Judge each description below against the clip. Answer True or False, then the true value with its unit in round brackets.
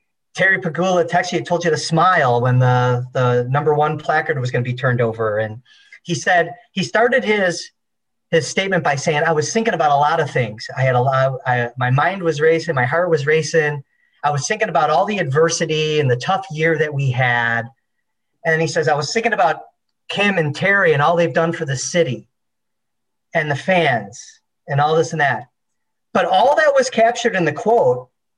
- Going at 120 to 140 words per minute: False (205 wpm)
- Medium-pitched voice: True (160 Hz)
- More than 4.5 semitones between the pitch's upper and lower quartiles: True (5.2 semitones)